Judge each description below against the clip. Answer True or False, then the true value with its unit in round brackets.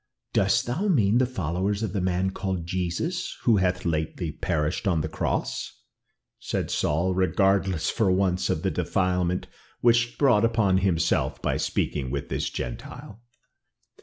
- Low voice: True (95 Hz)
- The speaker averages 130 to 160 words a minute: True (150 wpm)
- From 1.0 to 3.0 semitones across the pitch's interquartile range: False (3.7 semitones)